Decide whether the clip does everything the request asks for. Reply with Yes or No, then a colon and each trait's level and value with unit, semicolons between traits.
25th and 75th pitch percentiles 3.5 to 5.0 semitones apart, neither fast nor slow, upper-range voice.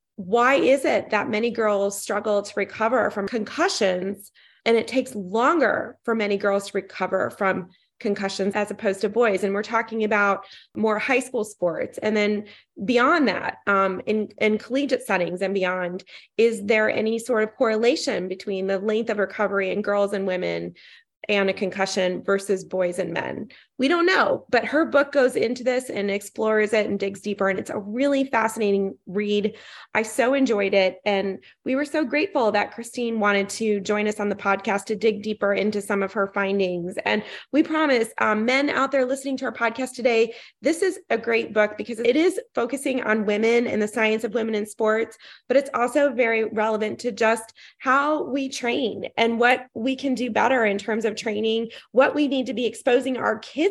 Yes: average, 3.8 semitones; average, 190 wpm; high, 220 Hz